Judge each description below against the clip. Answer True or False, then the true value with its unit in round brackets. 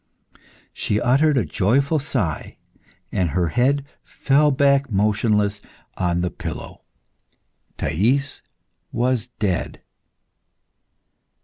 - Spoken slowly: True (90 wpm)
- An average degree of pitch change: False (6.4 semitones)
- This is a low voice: True (120 Hz)